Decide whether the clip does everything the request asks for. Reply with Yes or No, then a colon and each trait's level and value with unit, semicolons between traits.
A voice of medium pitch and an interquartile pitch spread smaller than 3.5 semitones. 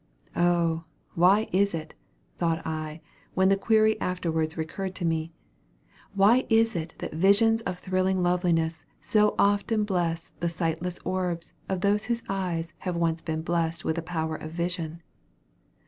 Yes: medium, 175 Hz; average, 3.0 semitones